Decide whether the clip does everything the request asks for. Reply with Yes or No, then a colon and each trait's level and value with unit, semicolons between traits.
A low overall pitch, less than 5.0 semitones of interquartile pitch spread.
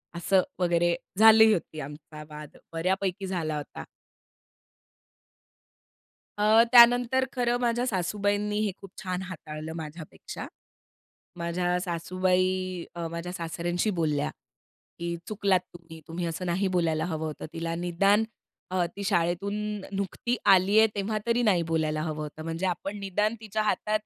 No: medium, 180 Hz; average, 3.5 semitones